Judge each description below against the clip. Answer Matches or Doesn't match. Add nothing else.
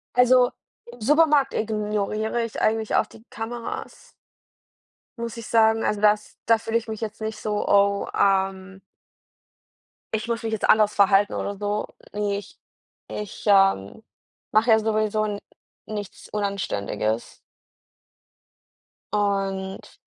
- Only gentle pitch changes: Matches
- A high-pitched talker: Matches